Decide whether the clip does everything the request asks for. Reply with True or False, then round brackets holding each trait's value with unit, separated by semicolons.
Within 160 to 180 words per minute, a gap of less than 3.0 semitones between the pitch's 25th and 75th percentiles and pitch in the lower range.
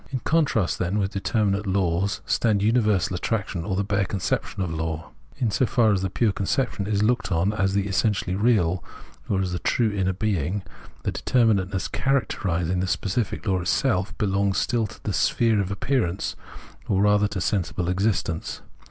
True (170 wpm; 2.6 semitones; 100 Hz)